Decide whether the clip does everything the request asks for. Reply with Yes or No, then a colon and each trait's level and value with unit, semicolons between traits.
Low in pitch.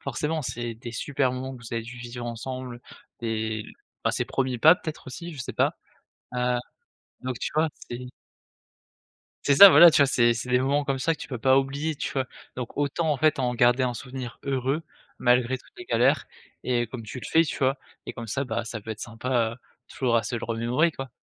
Yes: low, 125 Hz